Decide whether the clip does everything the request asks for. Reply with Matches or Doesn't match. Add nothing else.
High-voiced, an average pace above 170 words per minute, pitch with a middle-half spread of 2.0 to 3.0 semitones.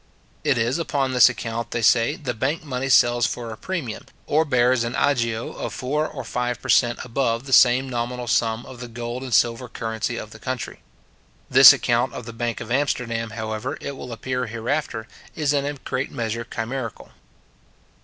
Doesn't match